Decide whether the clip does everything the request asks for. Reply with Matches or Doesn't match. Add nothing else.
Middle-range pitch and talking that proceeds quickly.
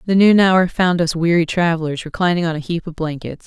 Matches